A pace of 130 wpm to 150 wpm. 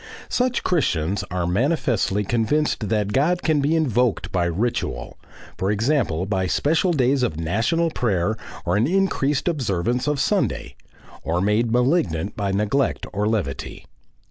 Yes: average, 140 wpm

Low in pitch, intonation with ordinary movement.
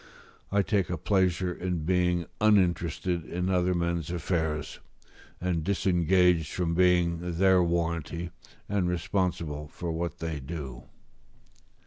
No: very low, 85 Hz; narrow, 1.7 semitones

